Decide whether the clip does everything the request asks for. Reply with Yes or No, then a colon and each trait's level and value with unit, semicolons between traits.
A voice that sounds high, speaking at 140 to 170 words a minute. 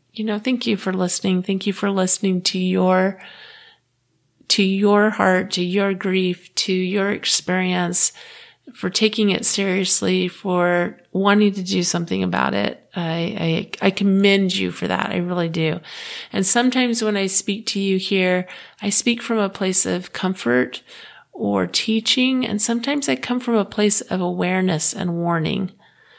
Yes: high, 195 Hz; average, 160 wpm